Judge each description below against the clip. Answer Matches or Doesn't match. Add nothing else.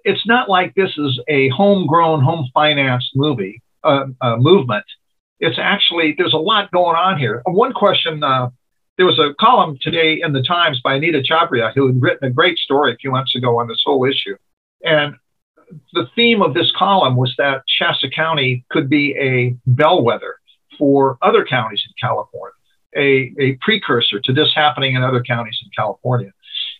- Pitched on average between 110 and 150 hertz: Matches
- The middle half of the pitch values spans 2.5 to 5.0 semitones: Matches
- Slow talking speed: Doesn't match